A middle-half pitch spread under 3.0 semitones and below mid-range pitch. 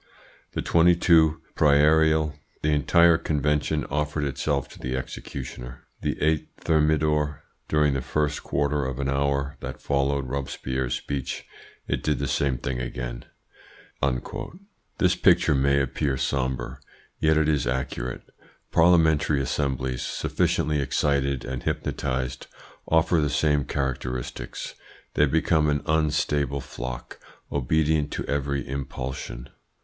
Yes: narrow, 2.5 semitones; very low, 70 Hz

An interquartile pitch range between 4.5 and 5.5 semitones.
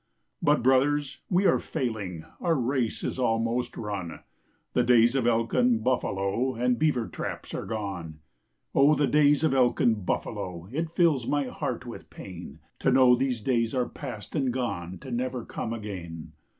No: average, 3.4 semitones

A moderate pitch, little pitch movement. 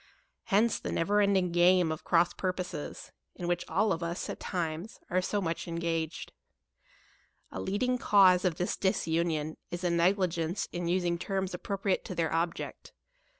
Yes: medium, 175 Hz; narrow, 2.2 semitones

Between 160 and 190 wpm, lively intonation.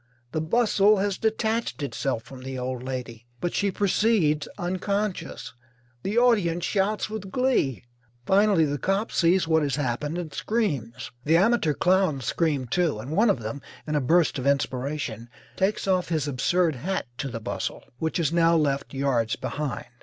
Yes: average, 165 wpm; wide, 6.2 semitones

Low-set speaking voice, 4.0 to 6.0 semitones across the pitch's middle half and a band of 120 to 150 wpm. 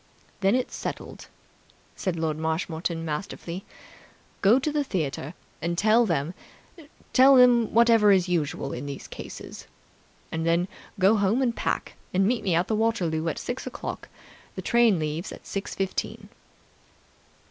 No: medium, 185 Hz; wide, 5.5 semitones; average, 140 wpm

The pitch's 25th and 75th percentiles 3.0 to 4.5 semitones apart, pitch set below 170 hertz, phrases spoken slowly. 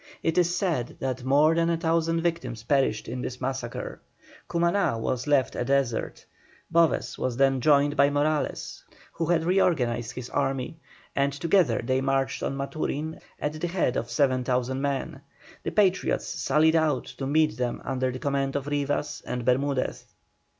No: average, 3.8 semitones; medium, 140 Hz; average, 160 wpm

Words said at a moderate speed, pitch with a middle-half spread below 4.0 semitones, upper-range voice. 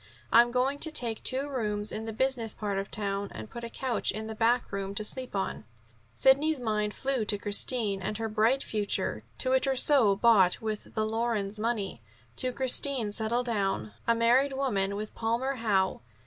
Yes: average, 180 wpm; average, 3.6 semitones; high, 225 Hz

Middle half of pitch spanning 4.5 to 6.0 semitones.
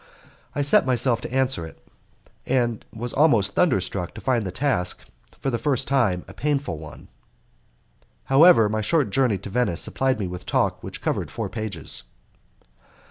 Yes: wide, 5.6 semitones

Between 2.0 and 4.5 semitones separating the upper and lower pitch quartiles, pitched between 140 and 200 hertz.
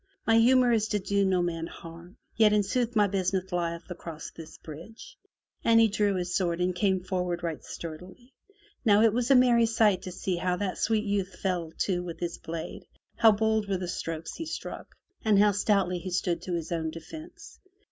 Yes: average, 3.8 semitones; high, 190 Hz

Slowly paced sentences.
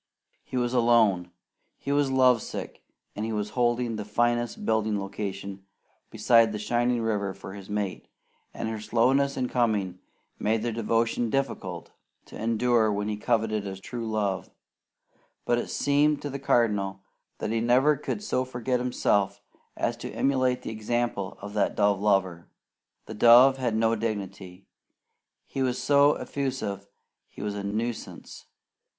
No: average, 155 wpm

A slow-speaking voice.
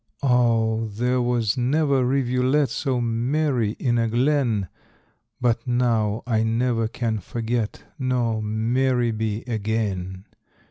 Yes: slow, 110 wpm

